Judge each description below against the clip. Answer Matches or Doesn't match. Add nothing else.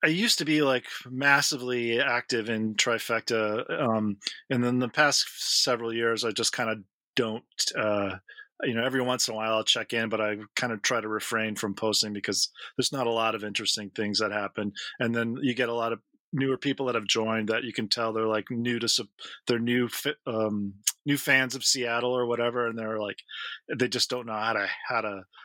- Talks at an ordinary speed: Doesn't match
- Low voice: Matches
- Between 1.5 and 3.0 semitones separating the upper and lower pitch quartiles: Matches